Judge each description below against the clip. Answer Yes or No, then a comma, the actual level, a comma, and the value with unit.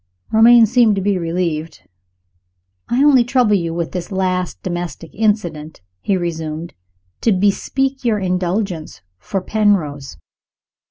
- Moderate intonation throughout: Yes, average, 4.5 semitones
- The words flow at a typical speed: No, slow, 120 wpm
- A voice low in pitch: No, medium, 185 Hz